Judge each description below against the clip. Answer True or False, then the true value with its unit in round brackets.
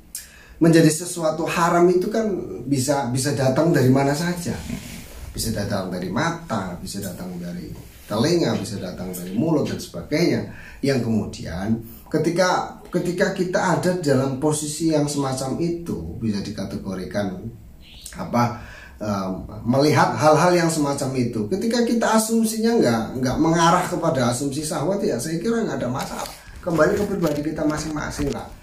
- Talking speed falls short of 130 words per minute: False (140 wpm)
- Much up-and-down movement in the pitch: True (7.2 semitones)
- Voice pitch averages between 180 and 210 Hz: False (150 Hz)